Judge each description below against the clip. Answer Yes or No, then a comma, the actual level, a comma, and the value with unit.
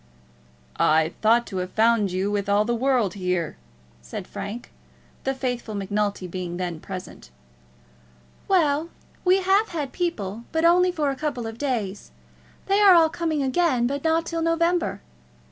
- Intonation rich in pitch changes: Yes, wide, 8.5 semitones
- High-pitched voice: Yes, high, 245 Hz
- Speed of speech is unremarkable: Yes, average, 155 wpm